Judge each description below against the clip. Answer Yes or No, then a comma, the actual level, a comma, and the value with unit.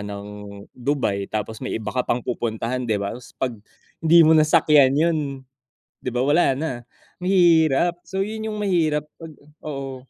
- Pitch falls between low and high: Yes, medium, 150 Hz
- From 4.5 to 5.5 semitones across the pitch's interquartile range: Yes, average, 5.2 semitones